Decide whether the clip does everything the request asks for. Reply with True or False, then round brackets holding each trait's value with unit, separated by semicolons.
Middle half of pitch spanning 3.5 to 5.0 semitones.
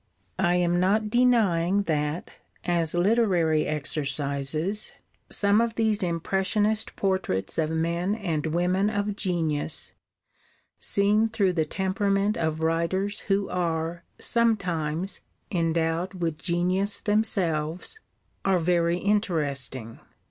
True (3.8 semitones)